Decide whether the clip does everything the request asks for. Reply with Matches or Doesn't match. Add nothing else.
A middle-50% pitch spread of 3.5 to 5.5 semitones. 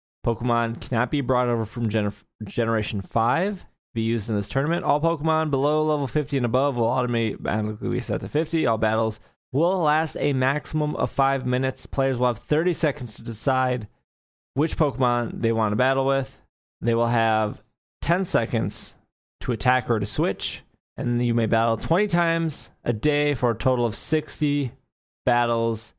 Matches